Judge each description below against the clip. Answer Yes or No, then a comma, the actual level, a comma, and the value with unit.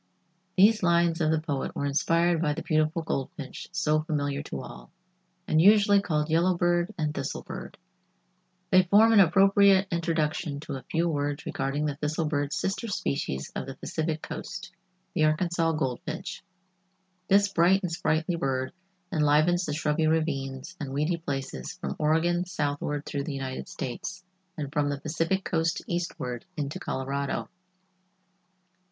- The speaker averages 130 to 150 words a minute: Yes, average, 145 wpm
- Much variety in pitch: No, average, 3.3 semitones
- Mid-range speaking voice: Yes, medium, 155 Hz